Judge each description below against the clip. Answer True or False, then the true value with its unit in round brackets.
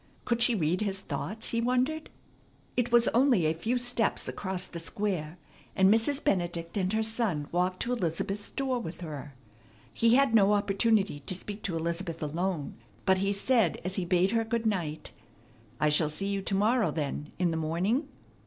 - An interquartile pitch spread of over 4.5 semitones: True (5.3 semitones)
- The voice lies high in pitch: True (195 Hz)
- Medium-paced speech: True (180 wpm)